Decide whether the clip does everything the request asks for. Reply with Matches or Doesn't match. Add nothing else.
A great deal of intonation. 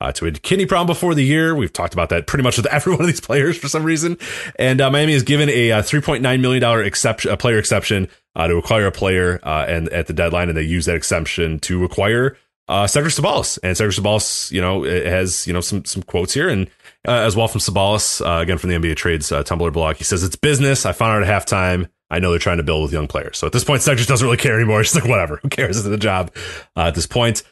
Matches